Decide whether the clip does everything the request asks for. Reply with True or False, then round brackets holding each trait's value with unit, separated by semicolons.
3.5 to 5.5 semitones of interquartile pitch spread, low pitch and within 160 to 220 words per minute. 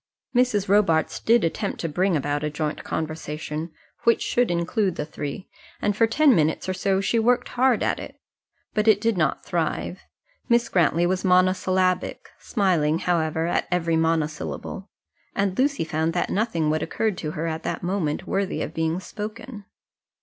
False (4.6 semitones; 185 Hz; 165 wpm)